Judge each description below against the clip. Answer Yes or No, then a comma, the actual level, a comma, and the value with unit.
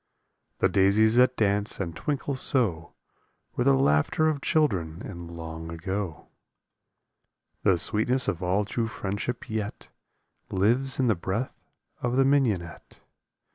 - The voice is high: No, low, 105 Hz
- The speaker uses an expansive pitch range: Yes, wide, 6.1 semitones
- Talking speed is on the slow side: Yes, slow, 130 wpm